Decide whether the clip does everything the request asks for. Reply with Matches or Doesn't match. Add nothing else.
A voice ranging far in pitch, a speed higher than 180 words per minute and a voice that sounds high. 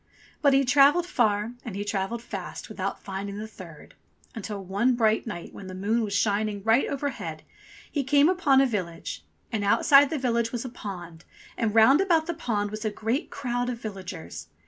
Doesn't match